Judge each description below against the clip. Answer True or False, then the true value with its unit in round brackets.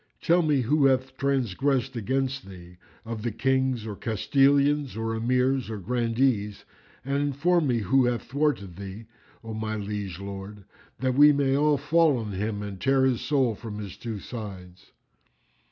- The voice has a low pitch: True (120 Hz)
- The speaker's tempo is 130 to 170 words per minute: True (160 wpm)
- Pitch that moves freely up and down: False (4.6 semitones)